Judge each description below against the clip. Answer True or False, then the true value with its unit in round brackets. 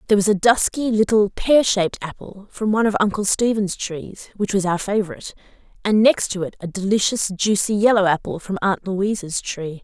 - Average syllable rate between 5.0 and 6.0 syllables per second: True (5.5 syllables/s)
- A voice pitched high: True (200 Hz)